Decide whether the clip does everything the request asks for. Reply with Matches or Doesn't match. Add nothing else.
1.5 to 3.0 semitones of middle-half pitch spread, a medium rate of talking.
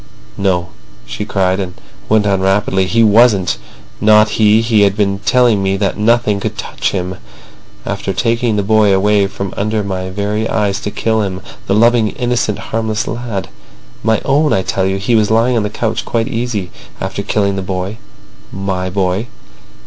Matches